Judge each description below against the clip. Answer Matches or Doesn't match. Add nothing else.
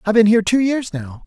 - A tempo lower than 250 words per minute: Doesn't match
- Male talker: Matches